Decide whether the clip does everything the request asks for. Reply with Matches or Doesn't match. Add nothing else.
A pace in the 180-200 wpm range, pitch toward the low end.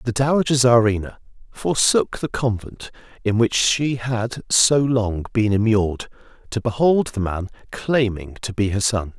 Doesn't match